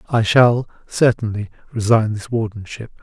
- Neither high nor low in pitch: No, low, 110 Hz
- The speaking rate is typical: No, slow, 120 wpm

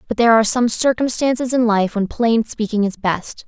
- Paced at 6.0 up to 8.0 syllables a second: No, 5.5 syllables/s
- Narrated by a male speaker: No, female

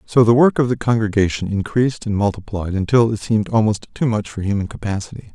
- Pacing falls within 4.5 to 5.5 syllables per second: No, 6.2 syllables/s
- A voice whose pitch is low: Yes, low, 110 Hz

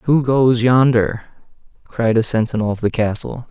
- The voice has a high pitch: No, low, 120 Hz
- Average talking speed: Yes, average, 155 wpm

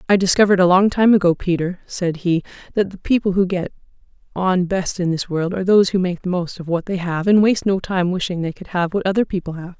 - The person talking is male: No, female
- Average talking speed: No, fast, 250 wpm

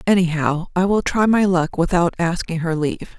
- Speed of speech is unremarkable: Yes, average, 190 wpm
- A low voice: No, medium, 175 Hz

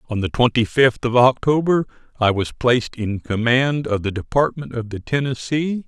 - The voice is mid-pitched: No, low, 125 Hz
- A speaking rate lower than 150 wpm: No, average, 175 wpm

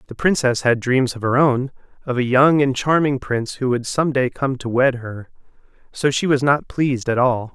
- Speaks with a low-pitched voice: Yes, low, 130 Hz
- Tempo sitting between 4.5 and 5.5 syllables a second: Yes, 5.0 syllables/s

